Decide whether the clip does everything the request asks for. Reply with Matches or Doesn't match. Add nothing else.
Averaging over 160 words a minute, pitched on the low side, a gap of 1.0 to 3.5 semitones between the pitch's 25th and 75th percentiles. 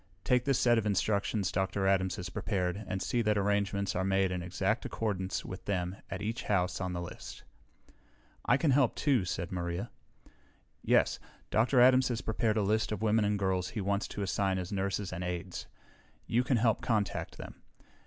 Matches